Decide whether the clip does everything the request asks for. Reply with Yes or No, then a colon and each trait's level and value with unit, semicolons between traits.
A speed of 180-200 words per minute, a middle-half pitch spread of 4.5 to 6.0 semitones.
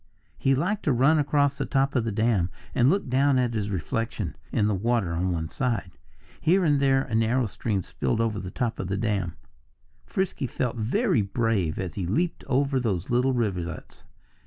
Yes: average, 190 wpm; average, 5.3 semitones